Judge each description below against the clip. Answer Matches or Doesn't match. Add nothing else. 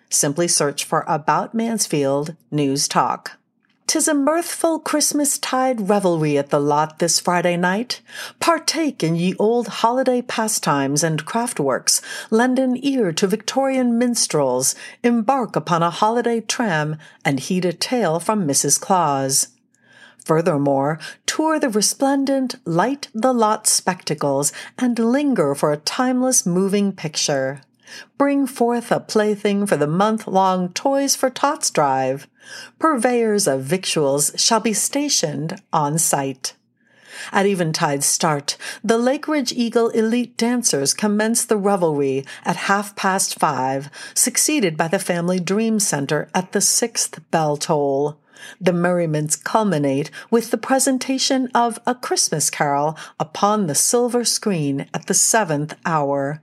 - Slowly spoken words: Matches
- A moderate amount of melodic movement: Doesn't match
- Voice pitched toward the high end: Matches